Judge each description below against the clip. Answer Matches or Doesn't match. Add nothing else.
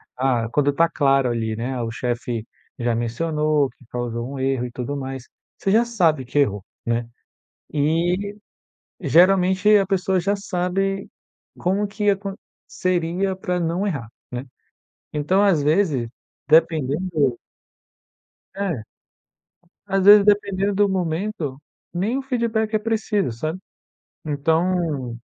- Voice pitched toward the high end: Doesn't match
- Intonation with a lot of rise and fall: Matches